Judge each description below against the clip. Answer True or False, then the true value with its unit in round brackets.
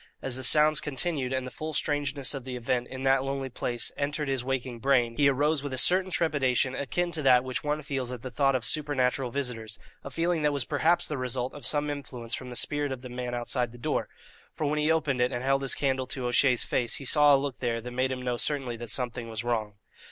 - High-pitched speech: False (130 Hz)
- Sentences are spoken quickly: True (245 wpm)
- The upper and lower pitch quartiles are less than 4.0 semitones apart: True (2.8 semitones)